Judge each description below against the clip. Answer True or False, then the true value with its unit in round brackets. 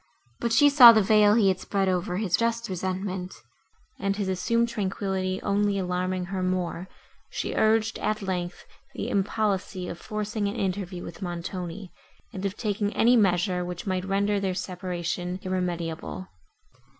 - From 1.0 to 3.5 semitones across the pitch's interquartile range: True (2.5 semitones)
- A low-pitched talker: False (190 Hz)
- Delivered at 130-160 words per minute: True (150 wpm)